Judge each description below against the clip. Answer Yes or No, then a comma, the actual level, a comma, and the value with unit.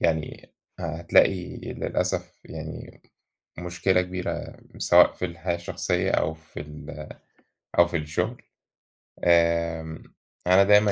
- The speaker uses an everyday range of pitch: No, narrow, 2.2 semitones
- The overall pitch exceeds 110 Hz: No, very low, 85 Hz